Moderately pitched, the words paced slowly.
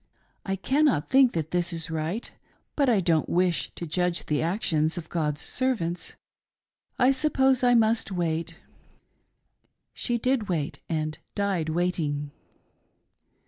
Yes: medium, 175 Hz; slow, 130 wpm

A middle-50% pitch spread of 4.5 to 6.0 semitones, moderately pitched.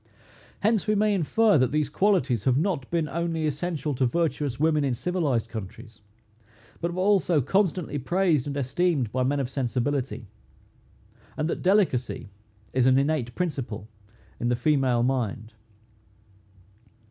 Yes: wide, 5.5 semitones; medium, 145 Hz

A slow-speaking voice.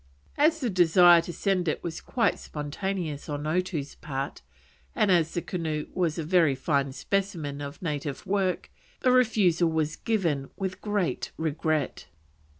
No: average, 150 wpm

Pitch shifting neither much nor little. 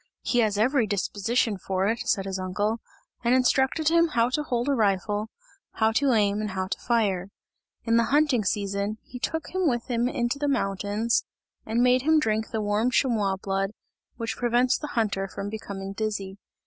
Yes: average, 3.7 semitones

